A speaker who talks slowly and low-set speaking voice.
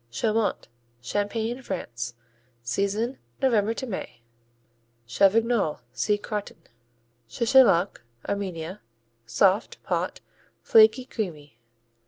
No: slow, 80 wpm; high, 205 Hz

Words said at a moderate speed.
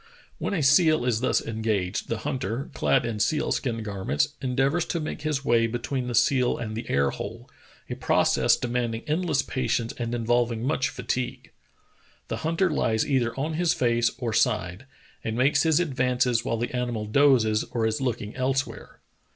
Yes: average, 175 wpm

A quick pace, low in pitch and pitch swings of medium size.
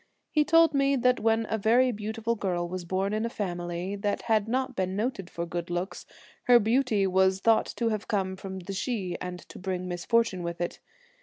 No: fast, 210 wpm; high, 200 Hz; average, 4.1 semitones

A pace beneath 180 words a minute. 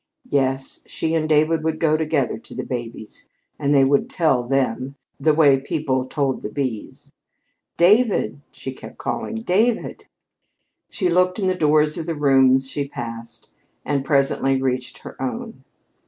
Yes: average, 155 wpm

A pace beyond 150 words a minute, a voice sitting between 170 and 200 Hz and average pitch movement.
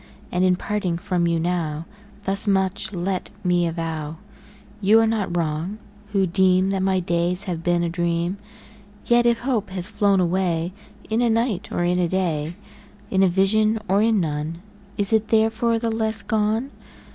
Yes: average, 170 wpm; high, 190 Hz; average, 3.7 semitones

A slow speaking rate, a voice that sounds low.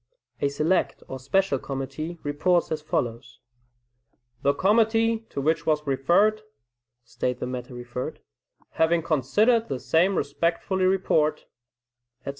No: slow, 120 wpm; medium, 155 Hz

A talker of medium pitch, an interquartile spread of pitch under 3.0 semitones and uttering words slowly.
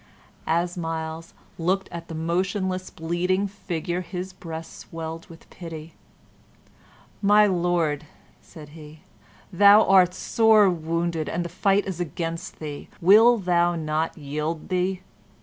Yes: medium, 175 Hz; narrow, 2.5 semitones; slow, 125 wpm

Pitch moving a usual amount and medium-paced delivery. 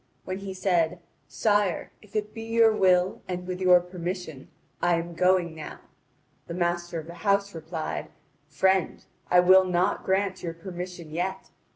No: narrow, 1.8 semitones; average, 160 wpm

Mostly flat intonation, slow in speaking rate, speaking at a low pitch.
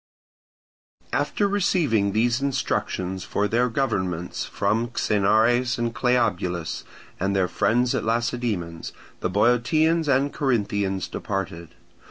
No: average, 4.4 semitones; slow, 105 wpm; low, 115 Hz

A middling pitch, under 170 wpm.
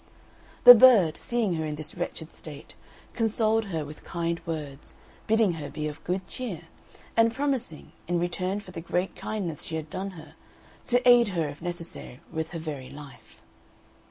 No: medium, 175 Hz; average, 175 wpm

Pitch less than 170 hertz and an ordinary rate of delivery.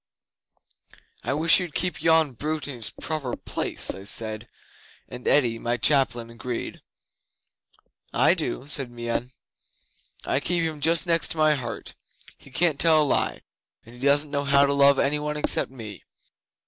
Yes: medium, 140 Hz; average, 160 wpm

